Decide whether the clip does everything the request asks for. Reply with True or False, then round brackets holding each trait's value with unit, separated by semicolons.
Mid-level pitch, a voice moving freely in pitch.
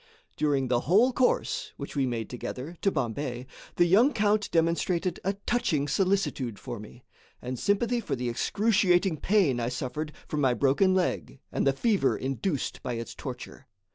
True (150 Hz; 7.5 semitones)